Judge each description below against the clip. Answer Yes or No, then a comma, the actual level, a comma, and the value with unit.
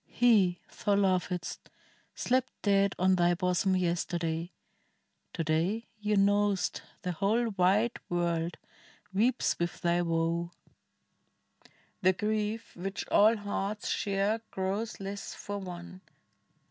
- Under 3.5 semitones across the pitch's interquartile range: Yes, average, 2.9 semitones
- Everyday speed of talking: No, slow, 110 wpm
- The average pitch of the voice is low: No, high, 195 Hz